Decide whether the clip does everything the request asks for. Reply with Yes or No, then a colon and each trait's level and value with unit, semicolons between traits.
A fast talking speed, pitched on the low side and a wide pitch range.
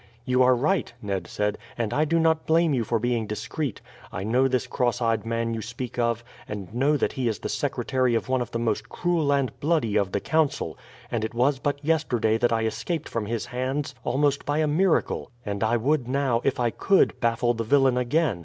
No: fast, 220 wpm; low, 125 Hz; average, 4.0 semitones